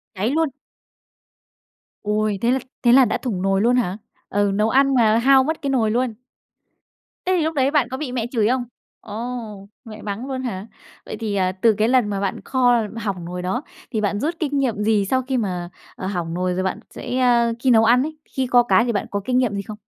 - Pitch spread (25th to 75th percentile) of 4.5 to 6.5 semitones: No, average, 4.0 semitones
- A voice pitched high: Yes, high, 230 Hz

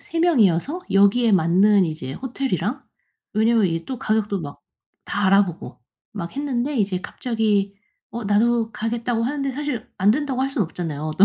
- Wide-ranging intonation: No, average, 4.8 semitones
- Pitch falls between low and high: No, high, 220 Hz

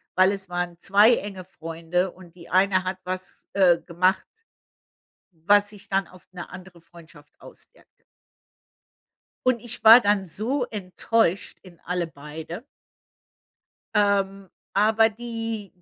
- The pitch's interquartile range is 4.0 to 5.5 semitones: No, average, 2.7 semitones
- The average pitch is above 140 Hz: Yes, high, 190 Hz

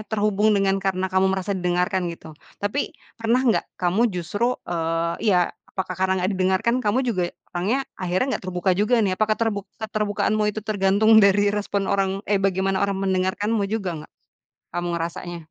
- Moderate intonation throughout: No, narrow, 2.3 semitones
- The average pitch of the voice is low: No, high, 195 Hz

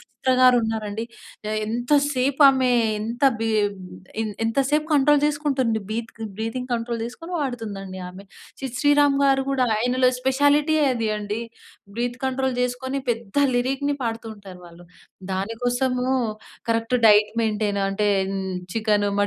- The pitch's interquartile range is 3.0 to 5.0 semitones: Yes, average, 3.5 semitones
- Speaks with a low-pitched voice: No, high, 240 Hz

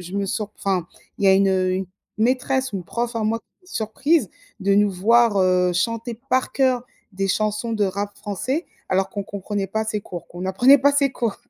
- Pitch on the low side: No, high, 210 Hz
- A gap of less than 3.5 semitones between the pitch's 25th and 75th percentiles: No, average, 3.8 semitones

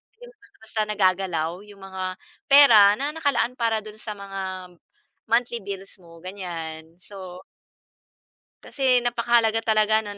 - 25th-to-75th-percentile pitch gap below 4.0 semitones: Yes, average, 3.6 semitones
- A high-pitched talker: Yes, high, 205 Hz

